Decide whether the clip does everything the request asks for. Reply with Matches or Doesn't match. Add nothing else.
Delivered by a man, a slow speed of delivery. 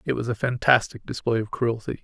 Doesn't match